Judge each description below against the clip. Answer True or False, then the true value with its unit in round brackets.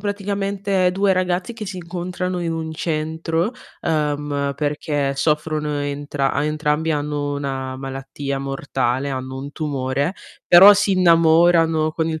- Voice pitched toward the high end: False (155 Hz)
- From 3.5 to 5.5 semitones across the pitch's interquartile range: True (3.8 semitones)